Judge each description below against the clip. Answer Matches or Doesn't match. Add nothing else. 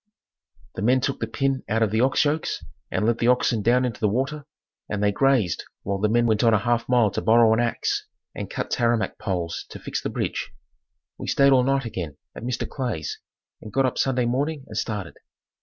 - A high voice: Doesn't match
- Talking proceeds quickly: Matches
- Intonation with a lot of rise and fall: Doesn't match